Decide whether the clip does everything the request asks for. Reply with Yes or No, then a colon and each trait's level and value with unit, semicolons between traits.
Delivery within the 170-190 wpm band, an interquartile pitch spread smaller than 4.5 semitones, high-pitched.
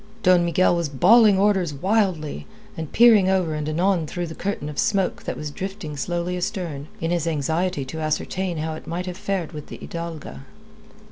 No: average, 185 wpm; average, 3.5 semitones; medium, 170 Hz